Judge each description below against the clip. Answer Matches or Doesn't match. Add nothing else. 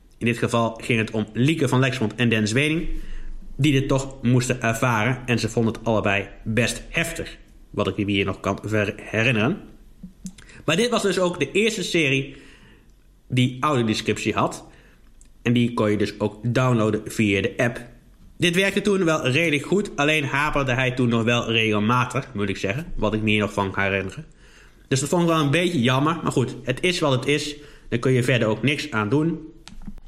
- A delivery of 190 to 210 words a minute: Matches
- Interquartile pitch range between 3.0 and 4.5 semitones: Doesn't match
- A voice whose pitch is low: Matches